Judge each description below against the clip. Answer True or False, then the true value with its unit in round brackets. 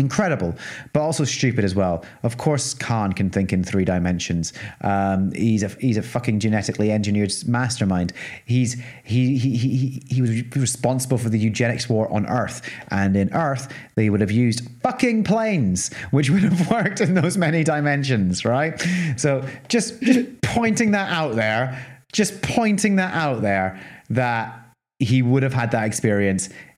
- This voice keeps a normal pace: True (160 wpm)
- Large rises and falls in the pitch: True (5.7 semitones)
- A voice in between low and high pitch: False (125 Hz)